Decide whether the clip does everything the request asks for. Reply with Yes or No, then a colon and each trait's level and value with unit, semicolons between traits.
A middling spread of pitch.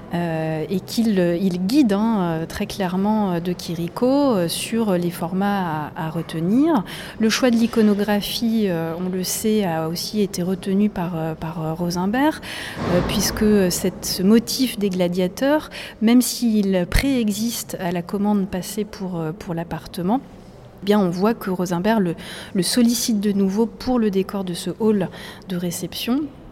Yes: average, 4.0 semitones